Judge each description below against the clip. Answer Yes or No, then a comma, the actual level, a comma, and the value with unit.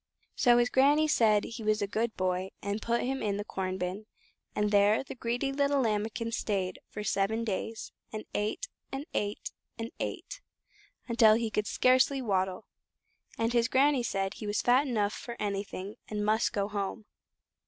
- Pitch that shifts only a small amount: No, average, 3.0 semitones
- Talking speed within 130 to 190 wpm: Yes, average, 175 wpm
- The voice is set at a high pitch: Yes, high, 215 Hz